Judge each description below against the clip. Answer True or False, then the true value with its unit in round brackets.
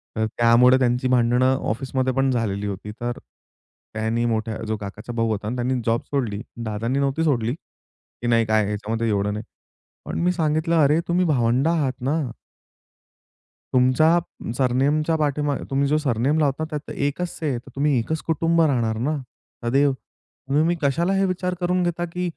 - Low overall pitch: True (130 Hz)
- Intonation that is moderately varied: True (4.9 semitones)